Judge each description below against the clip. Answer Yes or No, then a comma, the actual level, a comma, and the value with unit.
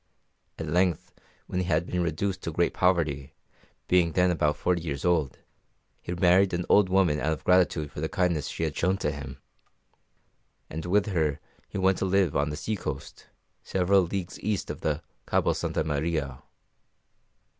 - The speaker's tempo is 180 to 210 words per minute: No, average, 170 wpm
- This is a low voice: Yes, very low, 85 Hz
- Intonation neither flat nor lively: Yes, average, 3.3 semitones